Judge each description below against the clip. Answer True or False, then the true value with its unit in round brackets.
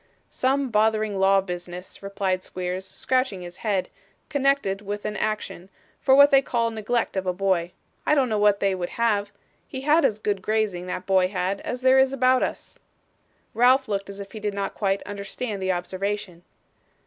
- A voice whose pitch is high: True (205 Hz)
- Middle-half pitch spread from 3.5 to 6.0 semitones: True (4.2 semitones)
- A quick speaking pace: False (185 wpm)